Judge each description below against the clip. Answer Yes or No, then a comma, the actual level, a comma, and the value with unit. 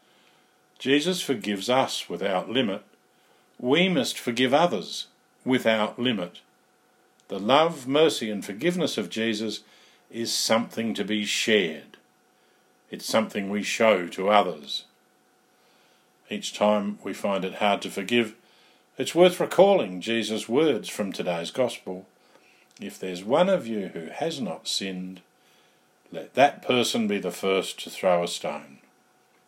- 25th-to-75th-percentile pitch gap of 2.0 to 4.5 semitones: No, average, 5.2 semitones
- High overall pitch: No, low, 110 Hz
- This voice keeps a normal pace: No, slow, 130 wpm